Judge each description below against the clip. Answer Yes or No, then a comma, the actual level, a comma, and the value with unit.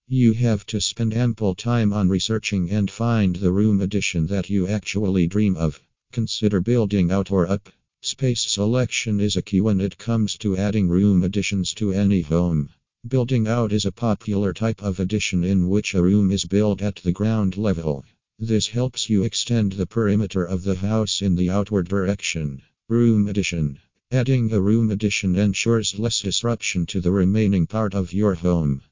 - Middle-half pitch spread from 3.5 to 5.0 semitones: No, average, 2.7 semitones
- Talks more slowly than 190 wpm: Yes, average, 175 wpm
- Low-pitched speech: Yes, low, 100 Hz